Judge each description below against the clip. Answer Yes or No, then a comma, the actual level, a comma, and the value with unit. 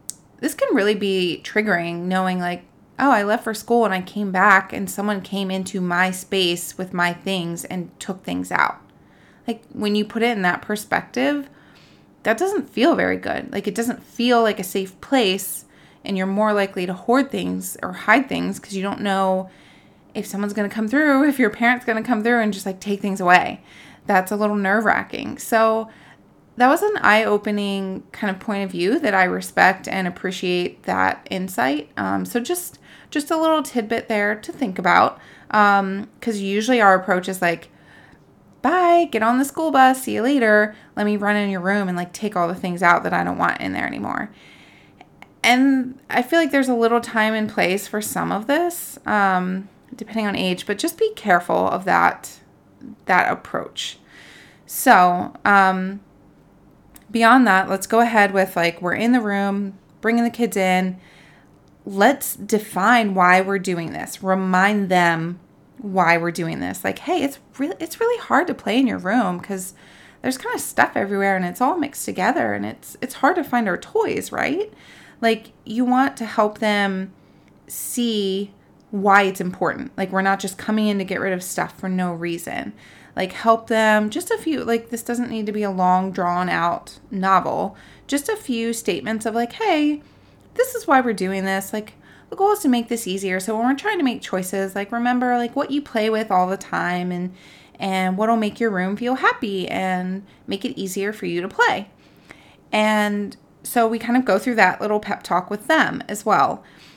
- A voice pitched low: No, high, 210 Hz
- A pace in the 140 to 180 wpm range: No, average, 195 wpm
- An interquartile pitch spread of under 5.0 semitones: Yes, average, 4.2 semitones